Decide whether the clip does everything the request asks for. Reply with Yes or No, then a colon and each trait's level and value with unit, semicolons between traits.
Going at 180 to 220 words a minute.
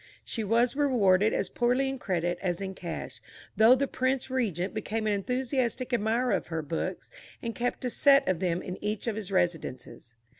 Yes: average, 185 wpm